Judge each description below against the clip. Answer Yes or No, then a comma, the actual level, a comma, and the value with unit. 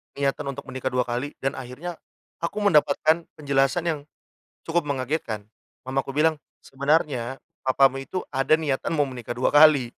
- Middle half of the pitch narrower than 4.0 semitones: Yes, average, 2.9 semitones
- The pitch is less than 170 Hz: Yes, medium, 140 Hz